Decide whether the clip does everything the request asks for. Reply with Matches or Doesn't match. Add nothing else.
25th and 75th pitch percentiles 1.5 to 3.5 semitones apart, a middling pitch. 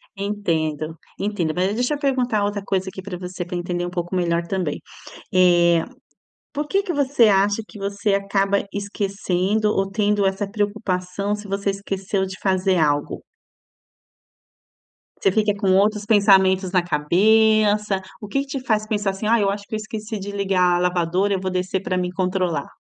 Doesn't match